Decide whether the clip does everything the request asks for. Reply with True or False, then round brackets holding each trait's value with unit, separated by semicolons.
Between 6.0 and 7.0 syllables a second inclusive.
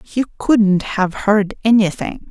False (4.0 syllables/s)